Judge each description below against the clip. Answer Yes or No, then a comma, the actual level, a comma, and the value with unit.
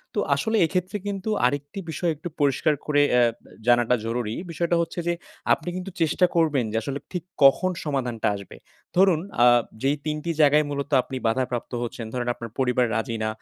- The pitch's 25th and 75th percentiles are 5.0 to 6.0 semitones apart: Yes, wide, 5.6 semitones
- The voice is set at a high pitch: No, medium, 145 Hz